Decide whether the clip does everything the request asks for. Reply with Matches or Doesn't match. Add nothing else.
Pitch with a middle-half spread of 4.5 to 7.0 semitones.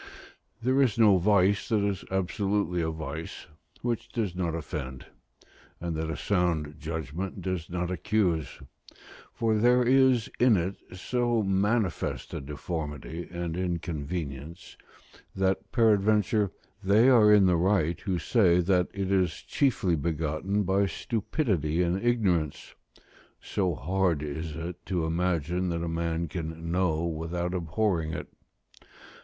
Doesn't match